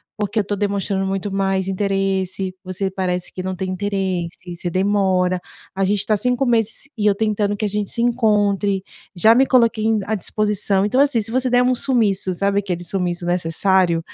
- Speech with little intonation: Yes, narrow, 2.2 semitones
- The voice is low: No, high, 200 Hz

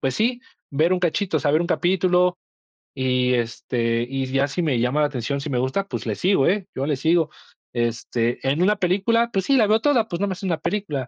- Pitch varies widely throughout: Yes, wide, 6.5 semitones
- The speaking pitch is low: No, medium, 160 Hz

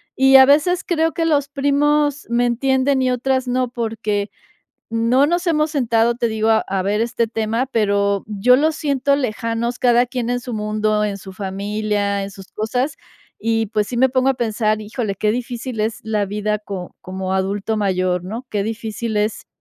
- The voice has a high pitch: Yes, high, 230 Hz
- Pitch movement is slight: No, average, 3.6 semitones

